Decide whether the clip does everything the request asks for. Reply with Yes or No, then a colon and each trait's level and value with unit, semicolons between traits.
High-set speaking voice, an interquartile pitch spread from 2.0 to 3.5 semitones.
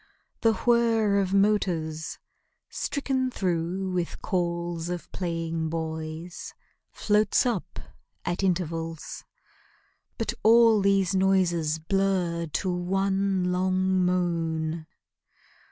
No: medium, 180 Hz; average, 2.8 semitones